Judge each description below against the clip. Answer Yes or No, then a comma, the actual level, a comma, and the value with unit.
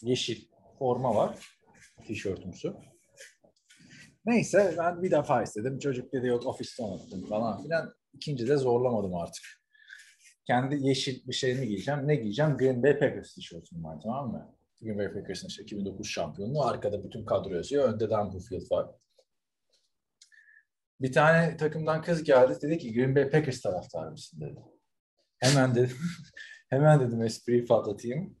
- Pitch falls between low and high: No, low, 130 Hz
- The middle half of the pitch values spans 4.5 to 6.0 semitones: Yes, average, 5.1 semitones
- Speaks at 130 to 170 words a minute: Yes, fast, 140 wpm